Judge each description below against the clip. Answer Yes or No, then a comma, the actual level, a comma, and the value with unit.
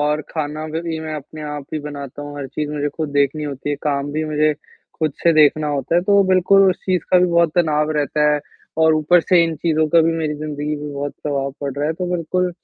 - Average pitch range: No, narrow, 2.1 semitones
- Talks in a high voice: No, medium, 155 Hz